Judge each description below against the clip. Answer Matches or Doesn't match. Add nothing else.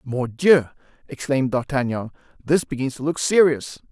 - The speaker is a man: Matches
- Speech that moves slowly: Matches